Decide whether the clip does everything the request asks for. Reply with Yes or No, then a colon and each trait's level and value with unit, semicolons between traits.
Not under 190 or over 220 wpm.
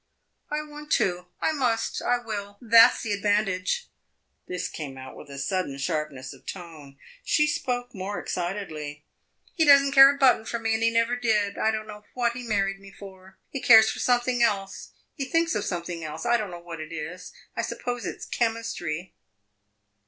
Yes: average, 195 wpm